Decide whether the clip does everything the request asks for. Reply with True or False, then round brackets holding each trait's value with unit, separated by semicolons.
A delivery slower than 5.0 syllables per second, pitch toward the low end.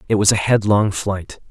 True (4.7 syllables/s; 100 Hz)